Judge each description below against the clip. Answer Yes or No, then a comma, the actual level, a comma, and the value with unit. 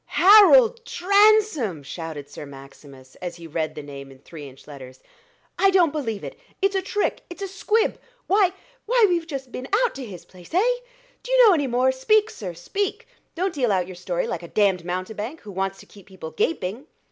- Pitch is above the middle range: Yes, high, 225 Hz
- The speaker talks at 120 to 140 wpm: No, average, 195 wpm